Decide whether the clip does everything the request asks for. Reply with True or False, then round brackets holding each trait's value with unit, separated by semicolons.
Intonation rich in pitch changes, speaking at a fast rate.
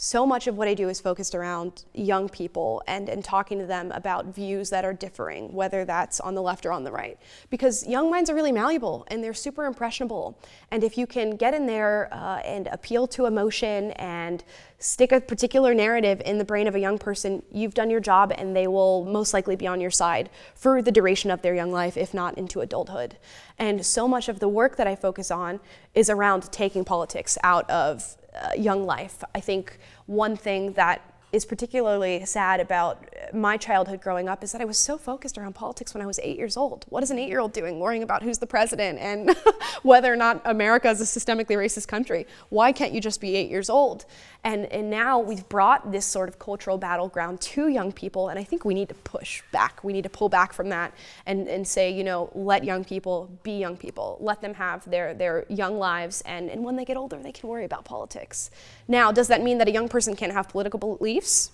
False (3.6 semitones; 225 wpm)